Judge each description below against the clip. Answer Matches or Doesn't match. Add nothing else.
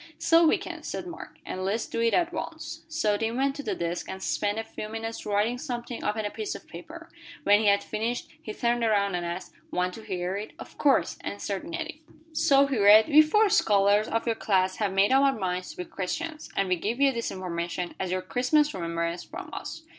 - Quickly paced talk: Matches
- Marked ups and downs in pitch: Matches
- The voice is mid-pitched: Doesn't match